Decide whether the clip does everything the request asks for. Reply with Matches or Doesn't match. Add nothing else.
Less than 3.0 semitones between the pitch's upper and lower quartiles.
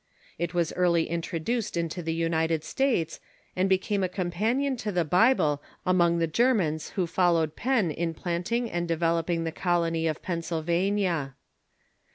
Matches